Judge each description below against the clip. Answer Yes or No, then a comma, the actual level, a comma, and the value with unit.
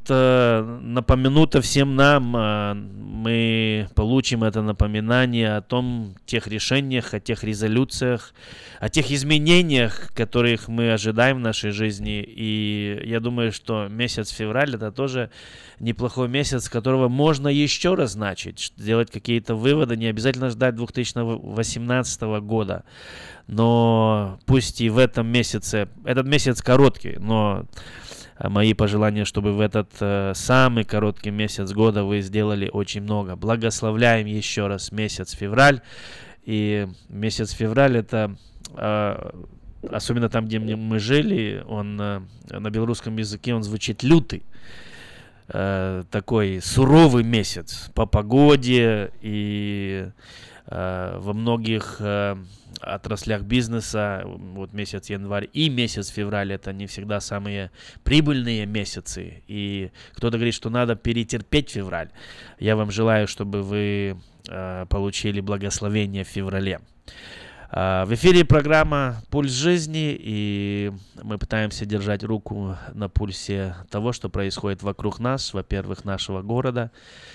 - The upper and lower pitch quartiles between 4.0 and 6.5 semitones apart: No, average, 2.9 semitones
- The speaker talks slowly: No, average, 120 wpm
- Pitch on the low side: Yes, low, 110 Hz